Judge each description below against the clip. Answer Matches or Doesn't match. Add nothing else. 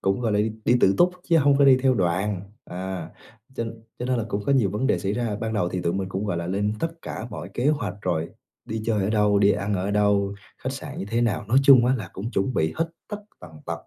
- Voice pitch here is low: Matches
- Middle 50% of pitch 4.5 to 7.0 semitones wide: Doesn't match